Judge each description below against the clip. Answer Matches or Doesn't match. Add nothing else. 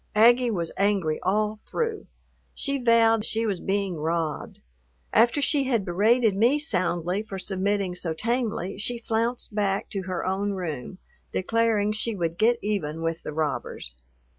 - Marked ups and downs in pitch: Doesn't match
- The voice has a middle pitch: Doesn't match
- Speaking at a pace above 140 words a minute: Matches